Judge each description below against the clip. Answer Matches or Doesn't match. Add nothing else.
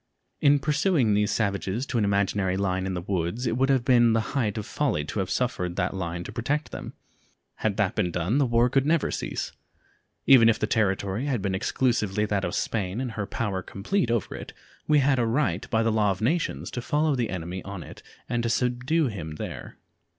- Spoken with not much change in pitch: Doesn't match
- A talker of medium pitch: Doesn't match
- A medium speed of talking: Doesn't match